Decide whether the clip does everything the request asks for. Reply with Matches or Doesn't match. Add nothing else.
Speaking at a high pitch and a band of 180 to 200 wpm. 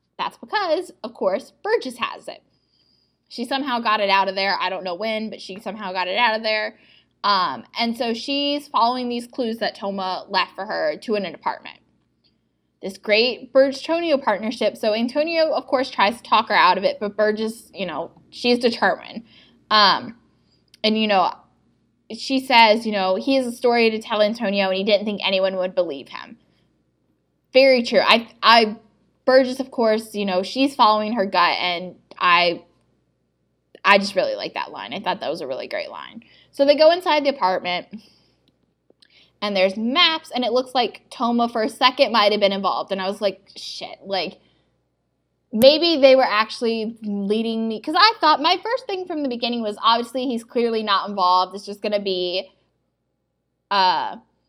Matches